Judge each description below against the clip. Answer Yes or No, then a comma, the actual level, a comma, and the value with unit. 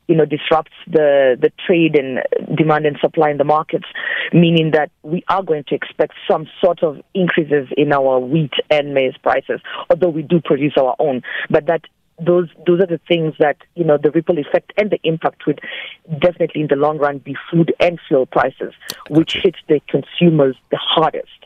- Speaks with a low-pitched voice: No, medium, 160 Hz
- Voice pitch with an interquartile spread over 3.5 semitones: No, average, 2.8 semitones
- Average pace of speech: Yes, average, 195 wpm